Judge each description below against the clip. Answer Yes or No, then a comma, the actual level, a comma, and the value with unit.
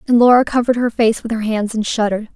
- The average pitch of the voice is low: No, high, 225 Hz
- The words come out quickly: Yes, fast, 255 wpm